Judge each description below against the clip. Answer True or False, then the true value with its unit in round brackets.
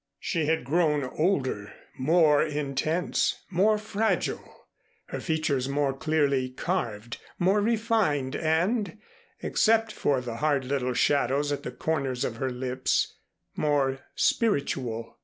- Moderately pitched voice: True (145 Hz)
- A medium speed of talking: False (120 wpm)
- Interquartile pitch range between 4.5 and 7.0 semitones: True (4.8 semitones)